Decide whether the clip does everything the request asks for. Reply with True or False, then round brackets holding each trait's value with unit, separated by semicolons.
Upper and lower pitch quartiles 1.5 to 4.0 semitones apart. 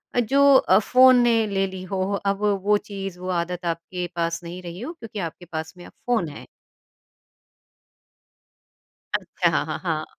False (4.4 semitones)